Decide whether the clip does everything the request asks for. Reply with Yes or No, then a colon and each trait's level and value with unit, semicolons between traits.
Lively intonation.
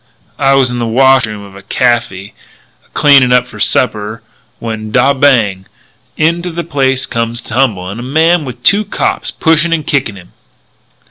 No: average, 4.5 semitones